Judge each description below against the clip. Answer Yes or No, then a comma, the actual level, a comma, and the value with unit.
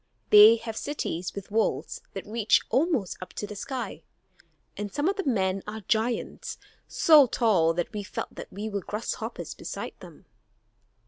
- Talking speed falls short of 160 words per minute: No, average, 170 wpm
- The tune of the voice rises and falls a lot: No, average, 3.4 semitones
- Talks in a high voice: Yes, high, 215 Hz